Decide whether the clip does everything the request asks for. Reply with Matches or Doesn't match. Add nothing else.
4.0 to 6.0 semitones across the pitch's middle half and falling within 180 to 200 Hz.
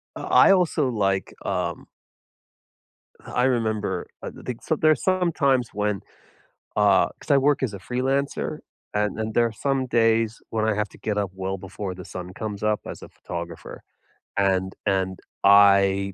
Doesn't match